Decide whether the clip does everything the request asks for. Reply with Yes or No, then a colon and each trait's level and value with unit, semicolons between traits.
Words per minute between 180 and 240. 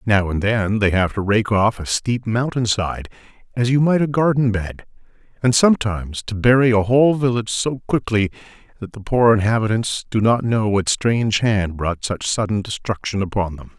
Yes: average, 185 wpm